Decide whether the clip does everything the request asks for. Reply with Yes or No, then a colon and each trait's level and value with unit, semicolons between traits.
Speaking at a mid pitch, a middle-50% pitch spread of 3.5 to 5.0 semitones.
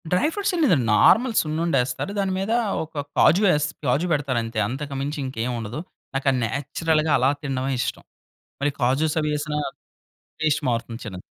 Yes: medium, 145 Hz; average, 3.9 semitones